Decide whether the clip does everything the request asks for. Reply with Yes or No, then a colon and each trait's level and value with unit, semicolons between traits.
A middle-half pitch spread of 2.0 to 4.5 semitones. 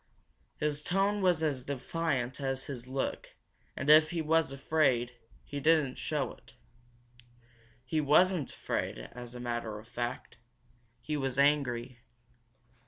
Yes: average, 4.1 semitones